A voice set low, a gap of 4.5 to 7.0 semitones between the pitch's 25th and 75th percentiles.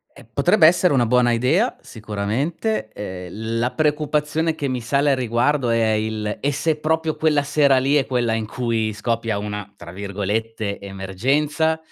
Yes: low, 120 Hz; wide, 5.5 semitones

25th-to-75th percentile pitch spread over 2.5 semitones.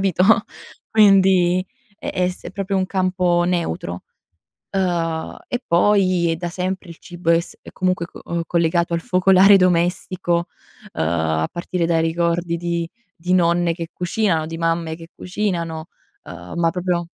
No: narrow, 1.7 semitones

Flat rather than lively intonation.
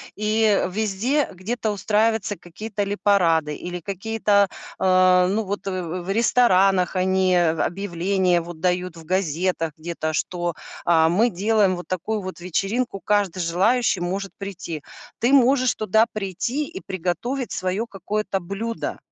No: average, 3.3 semitones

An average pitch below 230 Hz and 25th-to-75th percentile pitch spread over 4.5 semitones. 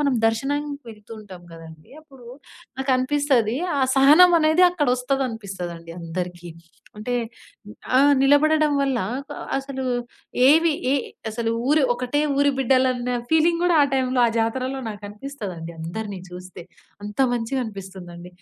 No: very high, 255 Hz; wide, 5.6 semitones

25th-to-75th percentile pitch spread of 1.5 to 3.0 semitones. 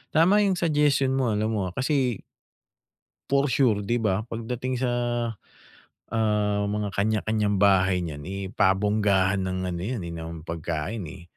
No: average, 4.6 semitones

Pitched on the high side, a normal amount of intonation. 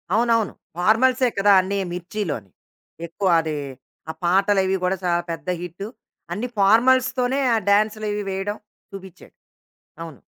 Yes: high, 200 Hz; average, 3.6 semitones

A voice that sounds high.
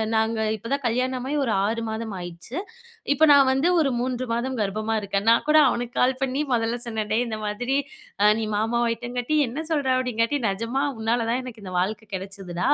Yes: high, 230 Hz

